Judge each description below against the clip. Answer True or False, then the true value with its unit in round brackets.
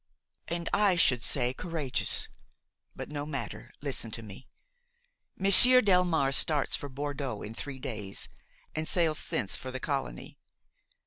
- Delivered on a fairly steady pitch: False (4.5 semitones)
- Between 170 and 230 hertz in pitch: False (140 Hz)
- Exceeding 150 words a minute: False (135 wpm)